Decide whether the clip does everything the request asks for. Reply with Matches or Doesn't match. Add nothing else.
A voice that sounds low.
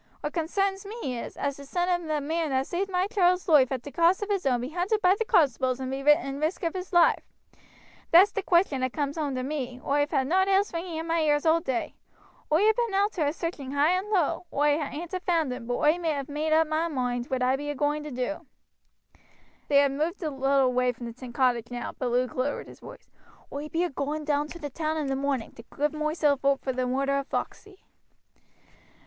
Doesn't match